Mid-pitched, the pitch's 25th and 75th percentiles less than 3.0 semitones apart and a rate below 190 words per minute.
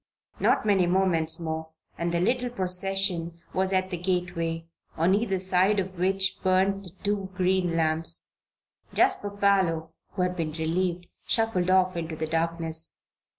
Yes: medium, 180 Hz; narrow, 2.5 semitones; average, 150 wpm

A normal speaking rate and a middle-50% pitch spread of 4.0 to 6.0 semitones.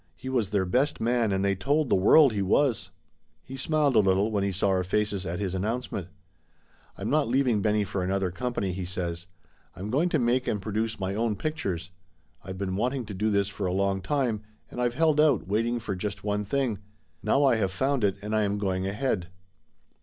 No: fast, 215 wpm; average, 4.4 semitones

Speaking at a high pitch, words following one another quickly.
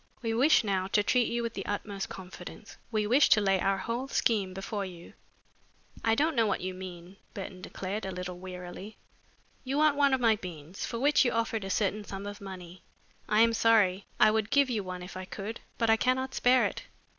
Yes: high, 205 Hz; fast, 215 wpm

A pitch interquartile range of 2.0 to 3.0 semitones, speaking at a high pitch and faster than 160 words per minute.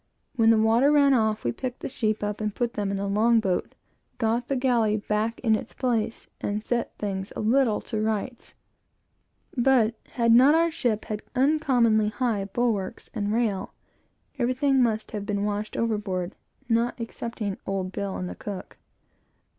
Yes: average, 2.7 semitones; high, 220 Hz; average, 170 wpm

